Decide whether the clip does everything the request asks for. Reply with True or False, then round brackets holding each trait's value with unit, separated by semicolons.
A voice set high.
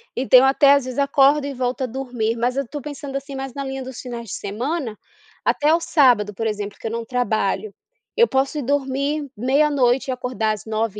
True (260 Hz)